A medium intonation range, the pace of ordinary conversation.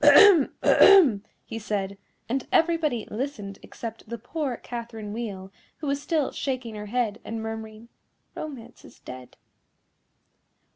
No: average, 4.7 semitones; slow, 130 wpm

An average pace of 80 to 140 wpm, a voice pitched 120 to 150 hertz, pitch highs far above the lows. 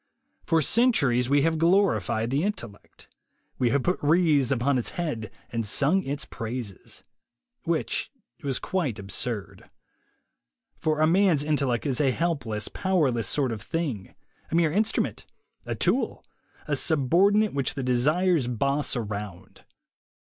Yes: slow, 135 wpm; medium, 140 Hz; wide, 5.7 semitones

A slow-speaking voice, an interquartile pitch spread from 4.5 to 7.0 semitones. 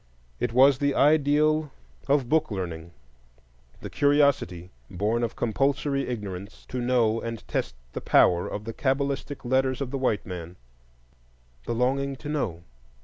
No: average, 145 wpm; average, 5.0 semitones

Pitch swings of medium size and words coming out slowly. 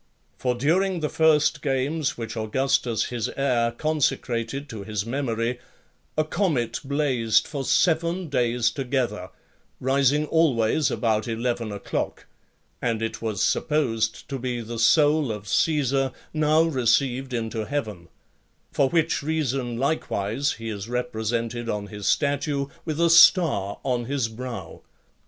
Yes: average, 4.4 semitones; slow, 130 wpm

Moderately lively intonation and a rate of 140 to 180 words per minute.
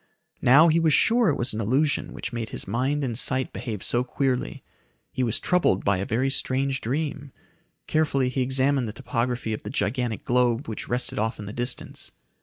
No: average, 3.2 semitones; average, 195 wpm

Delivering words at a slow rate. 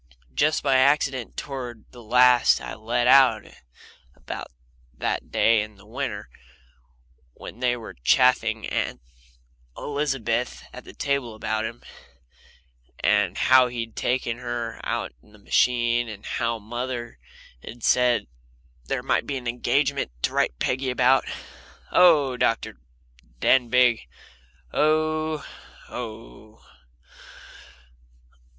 Yes: slow, 115 wpm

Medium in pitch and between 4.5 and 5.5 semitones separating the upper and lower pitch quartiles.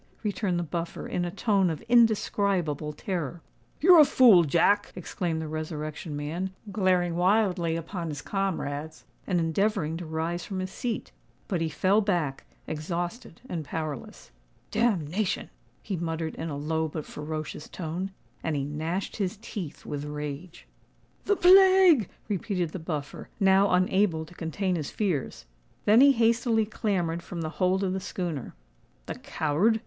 No: medium, 175 Hz; average, 4.1 semitones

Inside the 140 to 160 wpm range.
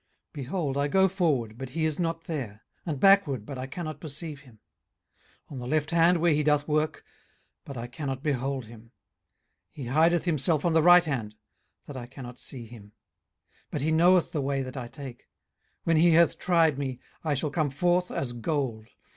No: average, 195 wpm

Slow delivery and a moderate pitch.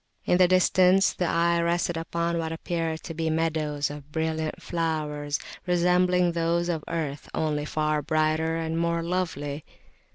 No: average, 150 wpm; medium, 165 Hz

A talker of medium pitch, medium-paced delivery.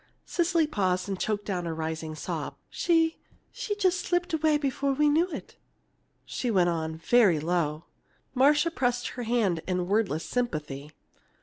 No: high, 220 Hz; average, 150 wpm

